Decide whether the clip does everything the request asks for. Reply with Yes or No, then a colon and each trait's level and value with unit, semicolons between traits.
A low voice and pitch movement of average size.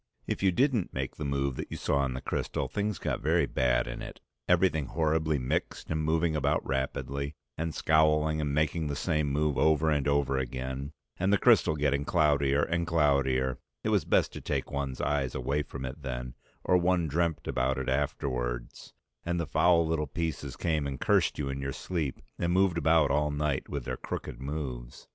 Yes: very low, 75 Hz; average, 3.0 semitones